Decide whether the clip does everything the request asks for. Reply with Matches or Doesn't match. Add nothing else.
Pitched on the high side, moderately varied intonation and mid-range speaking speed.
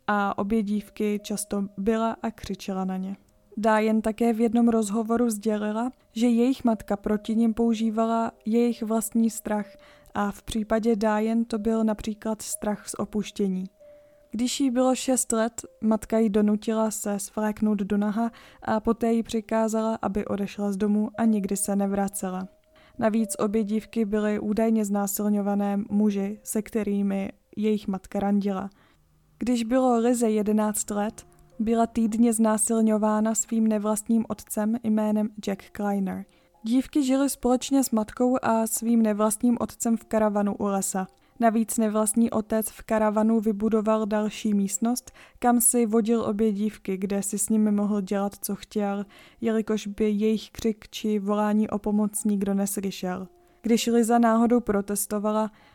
Doesn't match